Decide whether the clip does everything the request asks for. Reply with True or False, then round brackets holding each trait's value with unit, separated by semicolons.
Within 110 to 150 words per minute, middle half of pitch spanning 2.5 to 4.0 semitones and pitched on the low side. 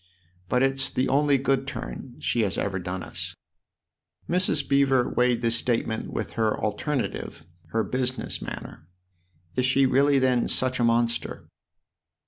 True (145 wpm; 3.0 semitones; 125 Hz)